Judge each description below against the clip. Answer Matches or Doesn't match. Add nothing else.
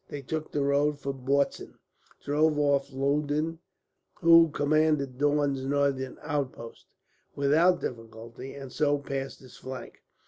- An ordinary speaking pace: Doesn't match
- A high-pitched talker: Doesn't match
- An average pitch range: Doesn't match